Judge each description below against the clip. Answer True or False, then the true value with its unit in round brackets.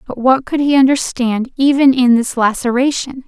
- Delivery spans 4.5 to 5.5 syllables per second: True (4.8 syllables/s)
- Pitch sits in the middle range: False (255 Hz)